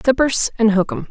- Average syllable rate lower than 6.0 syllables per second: No, 6.1 syllables/s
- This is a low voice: No, high, 235 Hz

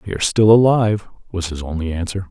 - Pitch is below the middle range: Yes, very low, 95 Hz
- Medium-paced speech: No, fast, 210 wpm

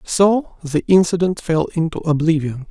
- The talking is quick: No, slow, 135 wpm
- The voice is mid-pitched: Yes, medium, 165 Hz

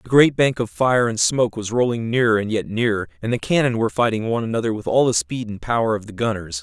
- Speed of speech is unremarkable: No, fast, 265 wpm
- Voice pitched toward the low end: Yes, low, 115 Hz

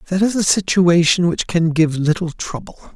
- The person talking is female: No, male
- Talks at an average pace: Yes, average, 185 wpm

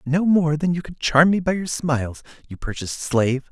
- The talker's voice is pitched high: No, medium, 150 Hz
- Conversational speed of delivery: No, fast, 220 wpm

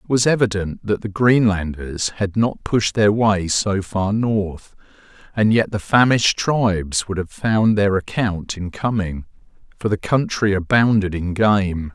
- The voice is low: Yes, low, 100 Hz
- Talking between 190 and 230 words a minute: No, average, 160 wpm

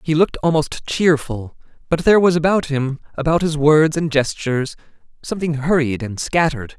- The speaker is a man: Yes, male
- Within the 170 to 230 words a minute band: No, average, 160 wpm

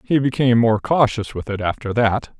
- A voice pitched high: No, low, 115 Hz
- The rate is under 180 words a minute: No, average, 200 wpm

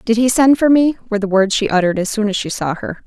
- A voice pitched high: Yes, high, 220 Hz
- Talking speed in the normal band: No, fast, 315 wpm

